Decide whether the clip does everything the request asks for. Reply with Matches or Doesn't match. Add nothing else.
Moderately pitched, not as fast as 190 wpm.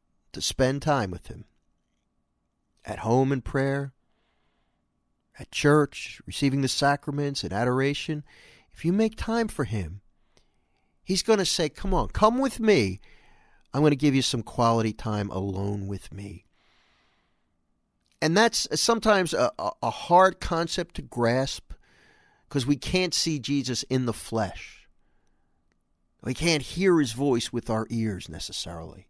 Doesn't match